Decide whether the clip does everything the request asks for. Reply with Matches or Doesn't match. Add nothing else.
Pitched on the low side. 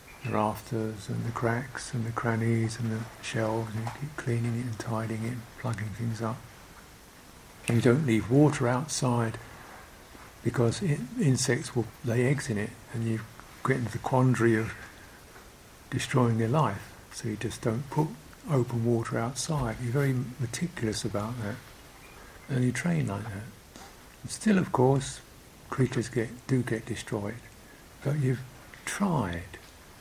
Matches